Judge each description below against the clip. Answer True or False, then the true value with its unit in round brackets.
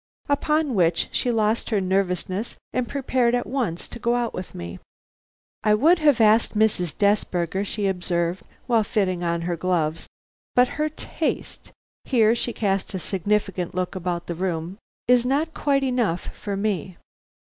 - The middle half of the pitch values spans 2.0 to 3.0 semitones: False (5.1 semitones)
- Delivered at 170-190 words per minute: False (155 wpm)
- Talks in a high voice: True (205 Hz)